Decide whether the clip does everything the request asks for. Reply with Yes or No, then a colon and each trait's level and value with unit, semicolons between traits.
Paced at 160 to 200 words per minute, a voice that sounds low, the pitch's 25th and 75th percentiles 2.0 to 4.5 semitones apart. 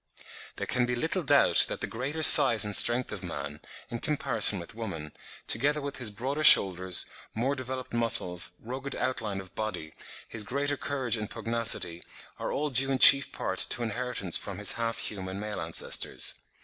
No: average, 175 wpm; low, 115 Hz; average, 5.0 semitones